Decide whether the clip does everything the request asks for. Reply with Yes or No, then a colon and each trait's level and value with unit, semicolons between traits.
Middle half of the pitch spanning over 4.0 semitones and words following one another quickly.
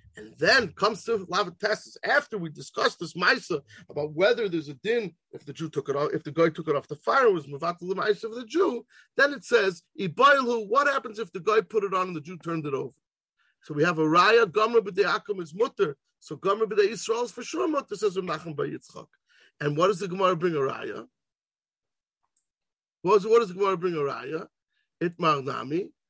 Yes: wide, 5.4 semitones; fast, 215 wpm